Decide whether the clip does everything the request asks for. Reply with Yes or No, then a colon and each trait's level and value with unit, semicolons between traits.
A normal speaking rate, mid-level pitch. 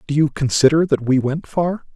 No: fast, 215 wpm; medium, 150 Hz